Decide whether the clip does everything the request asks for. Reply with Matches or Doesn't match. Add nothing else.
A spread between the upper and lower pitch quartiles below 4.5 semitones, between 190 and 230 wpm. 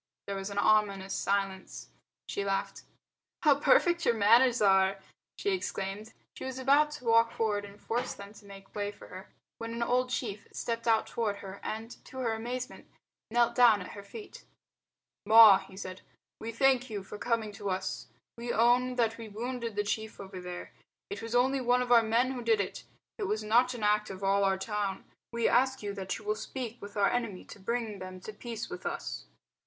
Matches